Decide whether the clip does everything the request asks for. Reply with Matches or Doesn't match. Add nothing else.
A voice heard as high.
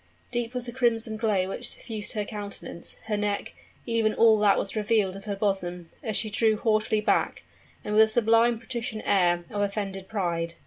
Matches